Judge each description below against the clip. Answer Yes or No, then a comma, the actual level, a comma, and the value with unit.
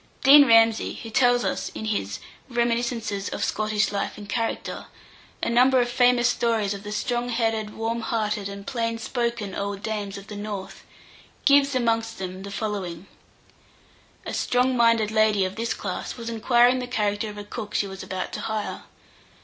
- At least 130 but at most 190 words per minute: Yes, average, 175 wpm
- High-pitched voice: Yes, high, 225 Hz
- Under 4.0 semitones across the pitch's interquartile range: Yes, narrow, 2.6 semitones